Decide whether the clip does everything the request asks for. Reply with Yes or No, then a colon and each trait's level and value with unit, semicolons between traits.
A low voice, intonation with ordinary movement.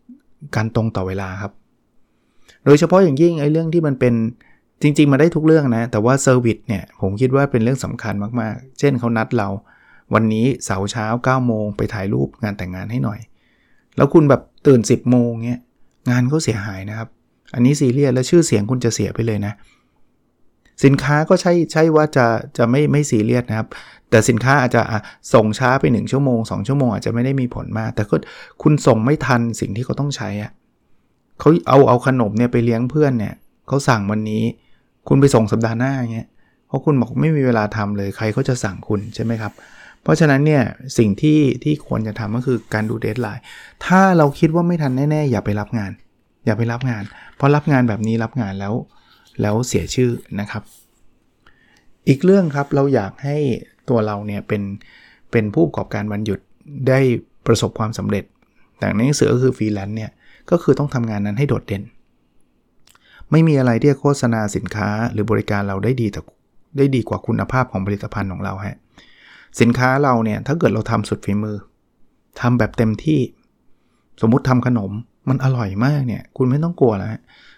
Yes: low, 120 Hz; average, 4.2 semitones